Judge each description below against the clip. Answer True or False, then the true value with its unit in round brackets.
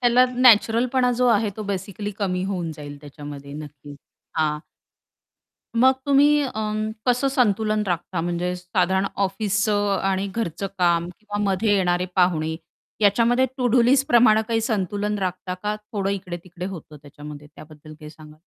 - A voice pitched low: False (195 Hz)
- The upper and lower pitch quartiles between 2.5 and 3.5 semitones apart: False (4.3 semitones)